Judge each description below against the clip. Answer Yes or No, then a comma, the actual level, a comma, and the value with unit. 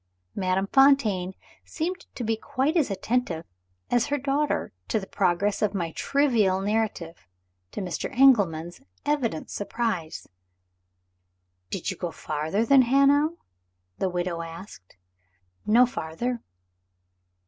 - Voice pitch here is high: Yes, high, 210 Hz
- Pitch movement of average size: No, wide, 7.0 semitones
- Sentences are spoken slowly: Yes, slow, 115 wpm